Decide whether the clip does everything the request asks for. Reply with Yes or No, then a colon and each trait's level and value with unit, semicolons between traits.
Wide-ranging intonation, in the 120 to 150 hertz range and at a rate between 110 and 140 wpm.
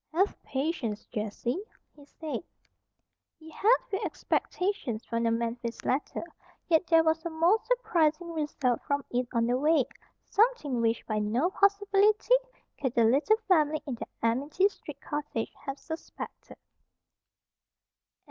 No: wide, 6.6 semitones; very high, 300 Hz; slow, 135 wpm